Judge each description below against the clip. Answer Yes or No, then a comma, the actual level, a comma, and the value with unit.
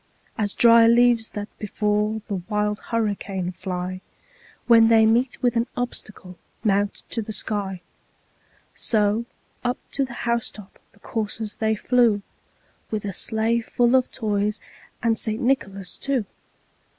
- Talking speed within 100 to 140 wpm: Yes, slow, 135 wpm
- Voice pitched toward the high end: Yes, high, 220 Hz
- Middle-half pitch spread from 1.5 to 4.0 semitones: Yes, narrow, 2.4 semitones